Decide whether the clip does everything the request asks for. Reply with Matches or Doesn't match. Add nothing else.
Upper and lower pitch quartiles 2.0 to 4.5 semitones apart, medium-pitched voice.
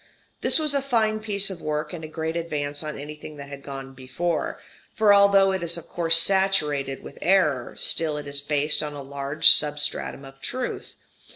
Doesn't match